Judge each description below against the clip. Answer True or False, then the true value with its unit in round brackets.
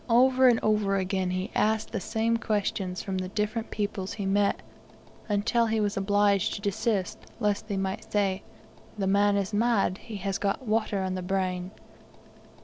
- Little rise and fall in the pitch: True (2.1 semitones)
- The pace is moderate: True (170 wpm)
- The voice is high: True (205 Hz)